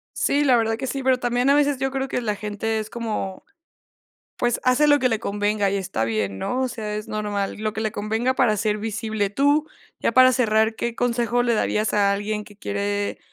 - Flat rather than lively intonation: No, average, 3.3 semitones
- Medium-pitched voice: No, high, 220 Hz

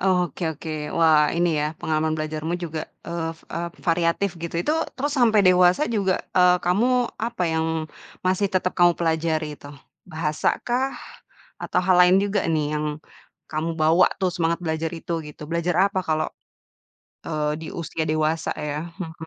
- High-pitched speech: No, medium, 170 Hz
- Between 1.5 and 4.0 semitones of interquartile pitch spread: Yes, narrow, 2.5 semitones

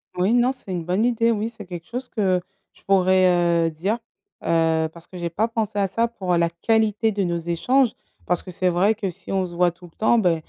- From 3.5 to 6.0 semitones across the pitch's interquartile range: Yes, average, 4.3 semitones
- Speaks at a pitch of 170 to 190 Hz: Yes, medium, 185 Hz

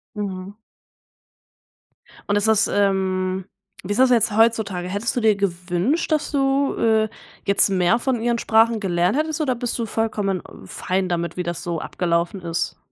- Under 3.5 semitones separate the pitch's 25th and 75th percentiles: No, average, 4.1 semitones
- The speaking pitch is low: No, high, 205 Hz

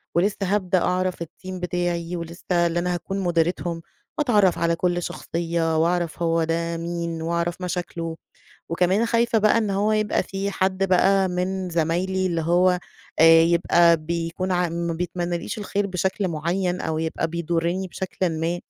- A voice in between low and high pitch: Yes, medium, 175 Hz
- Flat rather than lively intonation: Yes, narrow, 2.0 semitones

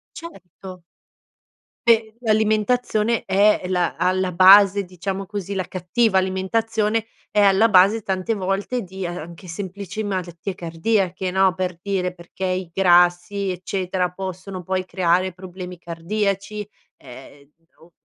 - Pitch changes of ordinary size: No, narrow, 2.2 semitones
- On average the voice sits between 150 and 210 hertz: Yes, high, 190 Hz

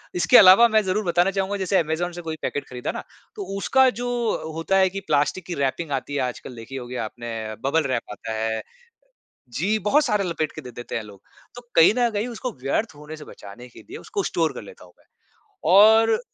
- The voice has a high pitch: No, medium, 165 Hz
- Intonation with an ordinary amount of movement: No, wide, 8.5 semitones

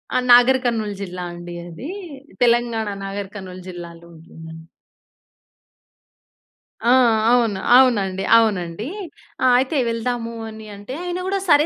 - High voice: Yes, high, 215 Hz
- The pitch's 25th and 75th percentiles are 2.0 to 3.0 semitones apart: No, average, 5.2 semitones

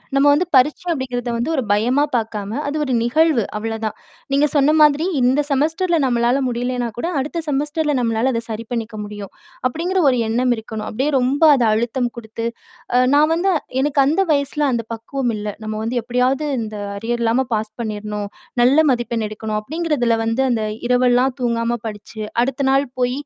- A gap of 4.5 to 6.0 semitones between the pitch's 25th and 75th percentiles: No, average, 3.8 semitones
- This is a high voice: Yes, high, 245 Hz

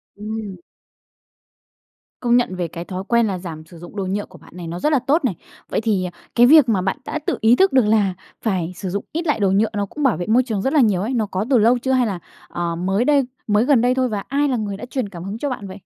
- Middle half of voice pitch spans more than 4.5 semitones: Yes, average, 4.9 semitones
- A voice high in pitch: Yes, high, 215 Hz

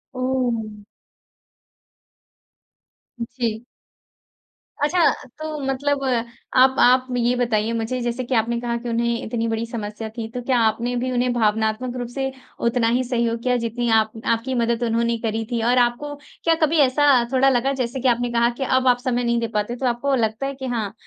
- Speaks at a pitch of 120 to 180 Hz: No, high, 240 Hz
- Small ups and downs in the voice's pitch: Yes, narrow, 1.8 semitones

